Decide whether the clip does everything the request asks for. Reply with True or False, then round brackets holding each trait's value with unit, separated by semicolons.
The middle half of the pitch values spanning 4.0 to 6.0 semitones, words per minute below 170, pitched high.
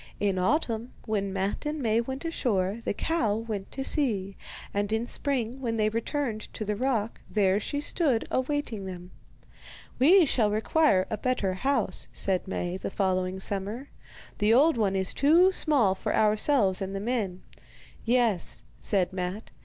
True (5.2 semitones; 160 wpm; 215 Hz)